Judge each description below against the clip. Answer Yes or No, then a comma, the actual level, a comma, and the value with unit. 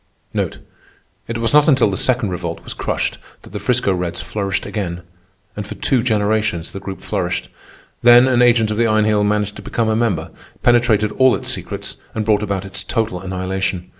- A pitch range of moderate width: Yes, average, 3.3 semitones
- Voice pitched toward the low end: Yes, low, 105 Hz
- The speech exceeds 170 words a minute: Yes, average, 190 wpm